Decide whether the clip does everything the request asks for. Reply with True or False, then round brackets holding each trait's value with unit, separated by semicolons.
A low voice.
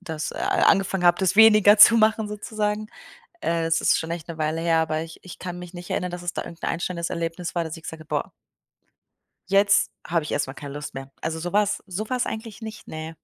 False (175 Hz)